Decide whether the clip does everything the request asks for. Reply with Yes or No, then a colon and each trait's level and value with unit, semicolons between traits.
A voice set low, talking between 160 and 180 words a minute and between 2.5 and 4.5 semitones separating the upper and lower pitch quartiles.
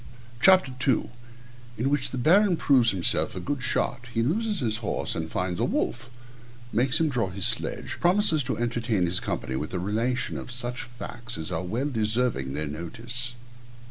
No: low, 120 Hz; average, 175 wpm; wide, 5.6 semitones